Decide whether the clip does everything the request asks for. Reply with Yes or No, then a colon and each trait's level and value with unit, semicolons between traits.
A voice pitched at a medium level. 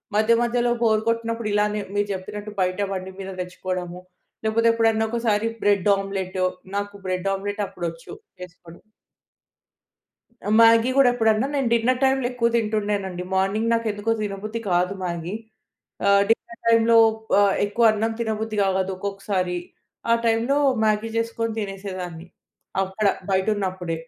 No: high, 205 Hz